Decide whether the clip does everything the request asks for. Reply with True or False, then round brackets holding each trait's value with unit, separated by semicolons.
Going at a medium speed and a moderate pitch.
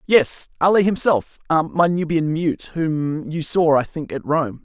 True (170 wpm; 160 Hz)